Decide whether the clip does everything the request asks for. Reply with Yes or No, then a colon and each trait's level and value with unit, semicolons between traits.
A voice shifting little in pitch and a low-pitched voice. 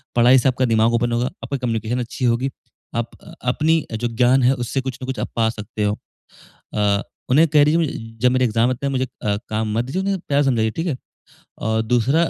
No: average, 3.0 semitones; low, 120 Hz